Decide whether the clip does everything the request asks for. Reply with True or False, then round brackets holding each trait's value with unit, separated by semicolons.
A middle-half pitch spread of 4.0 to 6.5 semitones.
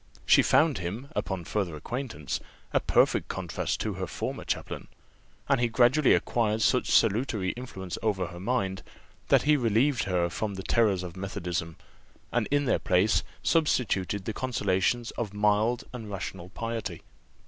True (4.3 semitones)